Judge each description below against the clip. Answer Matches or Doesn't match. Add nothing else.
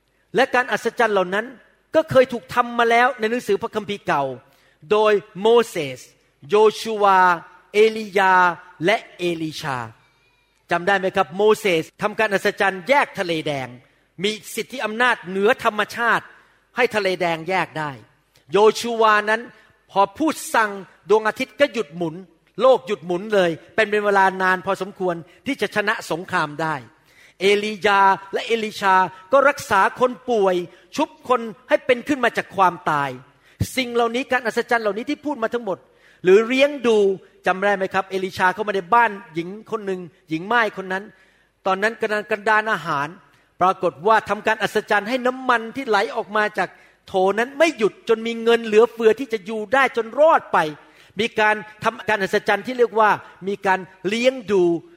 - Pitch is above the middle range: Matches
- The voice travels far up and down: Doesn't match